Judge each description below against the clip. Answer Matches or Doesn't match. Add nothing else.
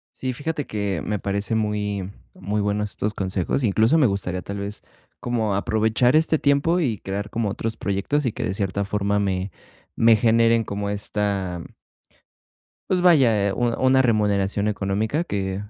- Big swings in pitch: Doesn't match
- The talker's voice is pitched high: Doesn't match